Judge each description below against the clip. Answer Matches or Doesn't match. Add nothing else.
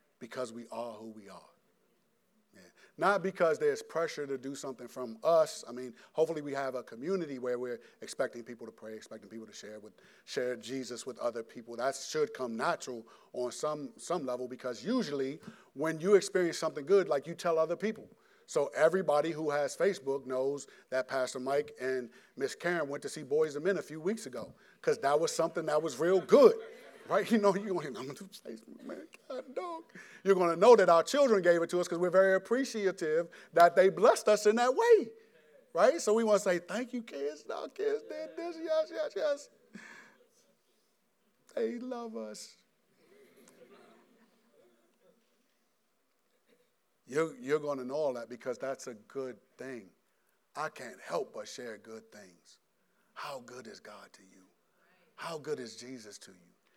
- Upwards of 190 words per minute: Doesn't match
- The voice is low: Doesn't match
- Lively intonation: Matches